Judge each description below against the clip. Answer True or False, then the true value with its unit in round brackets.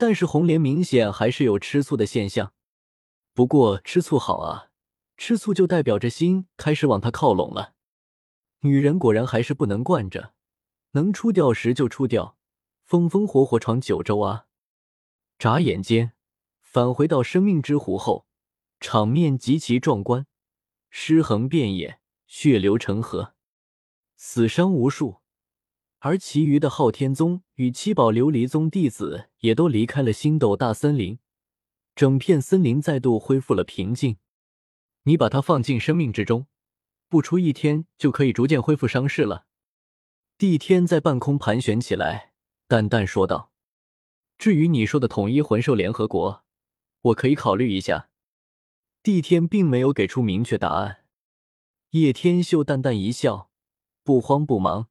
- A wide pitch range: True (6.2 semitones)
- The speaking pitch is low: True (130 Hz)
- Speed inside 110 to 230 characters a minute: True (220 characters per minute)